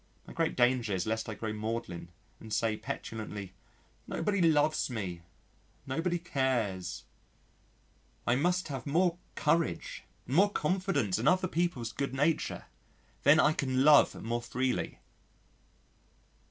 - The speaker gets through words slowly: Yes, slow, 125 wpm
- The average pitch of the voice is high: No, low, 130 Hz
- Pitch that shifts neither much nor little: No, wide, 6.7 semitones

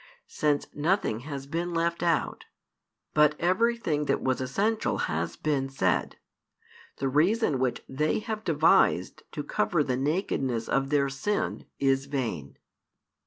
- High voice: No, medium, 150 Hz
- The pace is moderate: No, slow, 130 wpm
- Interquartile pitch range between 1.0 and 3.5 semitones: No, average, 4.5 semitones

